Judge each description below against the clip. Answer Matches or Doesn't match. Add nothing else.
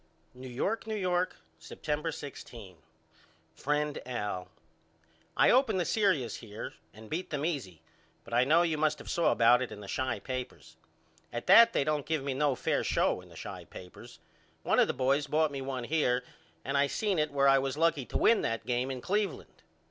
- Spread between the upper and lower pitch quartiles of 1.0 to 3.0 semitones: Doesn't match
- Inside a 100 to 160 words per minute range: Doesn't match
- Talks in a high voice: Doesn't match